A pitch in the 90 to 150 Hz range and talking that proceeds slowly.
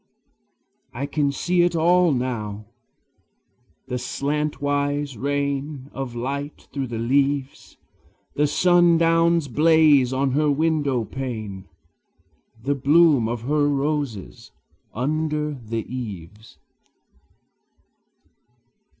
Yes: medium, 140 Hz; slow, 90 wpm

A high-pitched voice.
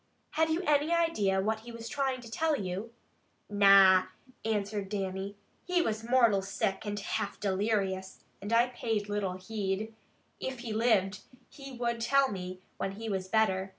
Yes: high, 215 Hz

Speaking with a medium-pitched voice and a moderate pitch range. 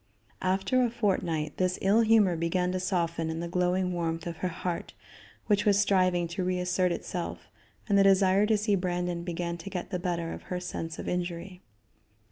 No: medium, 180 Hz; narrow, 2.0 semitones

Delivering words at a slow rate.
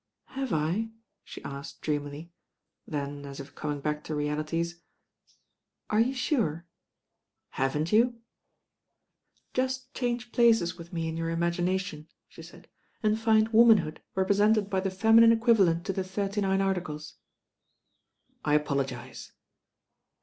Yes: slow, 130 wpm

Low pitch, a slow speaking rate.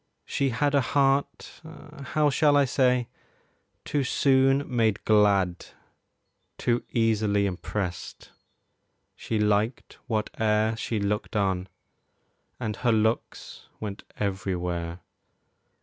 Yes: low, 110 Hz; slow, 100 wpm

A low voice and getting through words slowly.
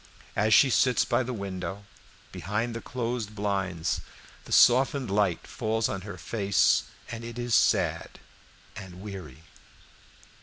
Yes: low, 105 Hz; slow, 130 wpm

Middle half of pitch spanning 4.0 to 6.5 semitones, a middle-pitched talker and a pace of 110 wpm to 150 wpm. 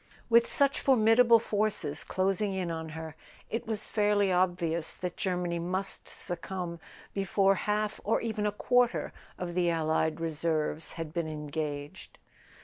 Yes: average, 4.3 semitones; medium, 180 Hz; average, 140 wpm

